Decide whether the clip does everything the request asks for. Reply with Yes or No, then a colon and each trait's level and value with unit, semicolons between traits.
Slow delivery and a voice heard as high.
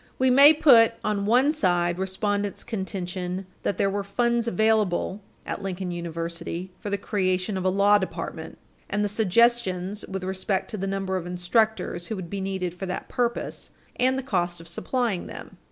No: average, 175 wpm; high, 195 Hz